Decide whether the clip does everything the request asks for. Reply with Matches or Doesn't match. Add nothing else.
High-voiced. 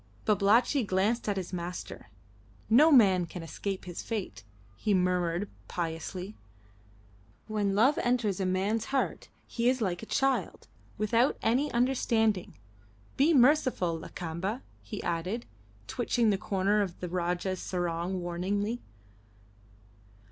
Matches